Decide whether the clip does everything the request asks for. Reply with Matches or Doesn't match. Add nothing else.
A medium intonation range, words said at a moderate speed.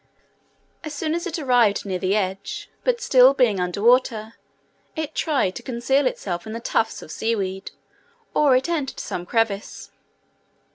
Doesn't match